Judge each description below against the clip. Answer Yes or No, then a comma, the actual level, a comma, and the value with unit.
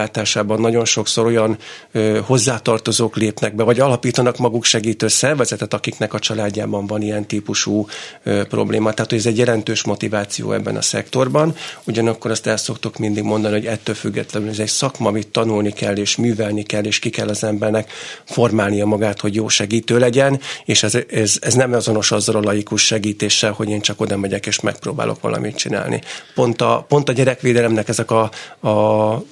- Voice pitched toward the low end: Yes, low, 110 Hz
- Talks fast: Yes, fast, 175 wpm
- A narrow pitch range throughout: Yes, narrow, 1.9 semitones